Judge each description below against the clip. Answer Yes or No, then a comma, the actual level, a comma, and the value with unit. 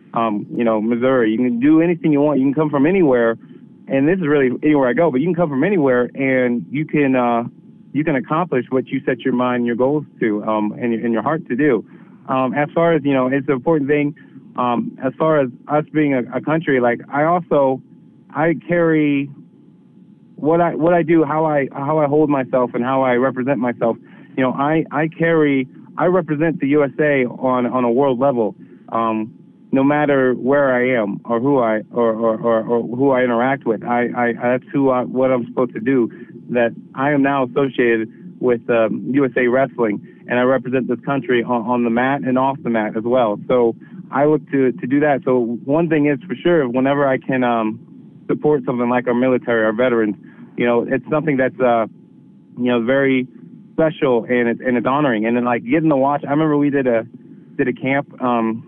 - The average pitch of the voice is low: Yes, low, 130 Hz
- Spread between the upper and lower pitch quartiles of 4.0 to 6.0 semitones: No, average, 3.3 semitones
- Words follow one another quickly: Yes, fast, 215 wpm